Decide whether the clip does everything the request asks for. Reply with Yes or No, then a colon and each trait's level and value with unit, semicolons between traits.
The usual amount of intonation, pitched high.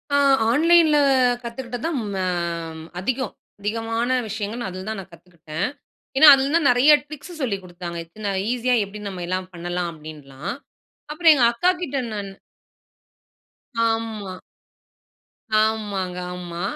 No: wide, 6.1 semitones; high, 215 Hz